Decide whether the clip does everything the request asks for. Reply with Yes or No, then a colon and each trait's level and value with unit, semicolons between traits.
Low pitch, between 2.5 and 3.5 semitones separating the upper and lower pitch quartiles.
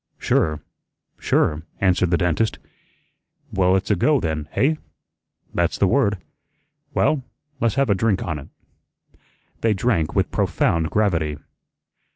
No: very low, 95 Hz; wide, 5.4 semitones